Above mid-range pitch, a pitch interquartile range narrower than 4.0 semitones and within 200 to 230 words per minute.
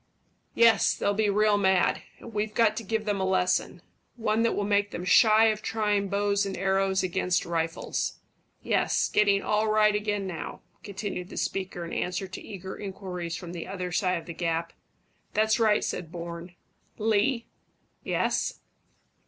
No: high, 200 Hz; average, 2.8 semitones; average, 165 wpm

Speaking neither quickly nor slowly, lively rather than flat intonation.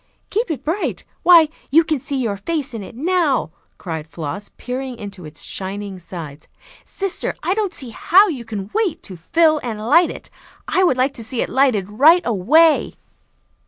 Yes: average, 180 wpm; wide, 8.4 semitones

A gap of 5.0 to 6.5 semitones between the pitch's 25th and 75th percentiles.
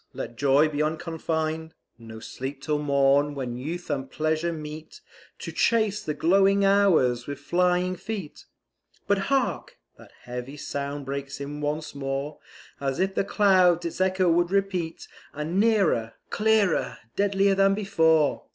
Yes: average, 5.3 semitones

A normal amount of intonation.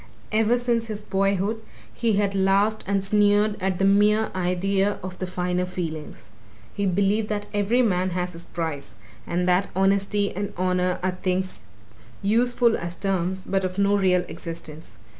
No: narrow, 2.3 semitones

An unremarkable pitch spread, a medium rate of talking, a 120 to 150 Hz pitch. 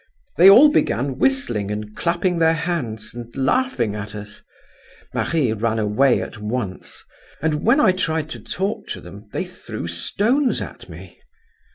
No: wide, 9.0 semitones; average, 155 wpm; low, 135 Hz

